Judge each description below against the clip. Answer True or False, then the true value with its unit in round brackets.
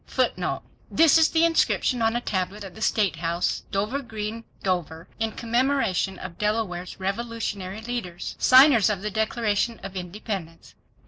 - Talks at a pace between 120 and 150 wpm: True (140 wpm)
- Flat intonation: False (4.0 semitones)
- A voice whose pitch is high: True (210 Hz)